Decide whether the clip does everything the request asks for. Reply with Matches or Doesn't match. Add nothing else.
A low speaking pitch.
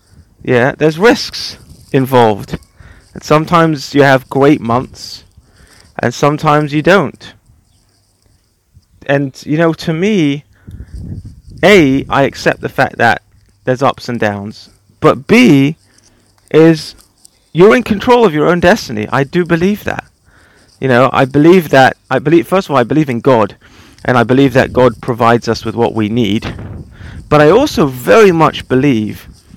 Matches